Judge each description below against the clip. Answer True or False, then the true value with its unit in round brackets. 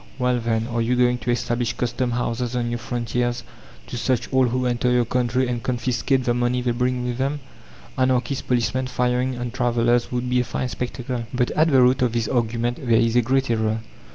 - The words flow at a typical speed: False (210 wpm)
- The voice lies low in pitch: True (125 Hz)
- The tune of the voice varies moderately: False (1.1 semitones)